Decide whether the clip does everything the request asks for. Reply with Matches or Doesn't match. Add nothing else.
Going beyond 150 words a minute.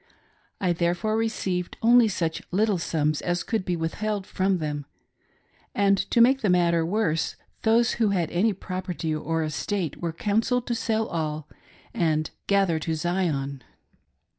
Doesn't match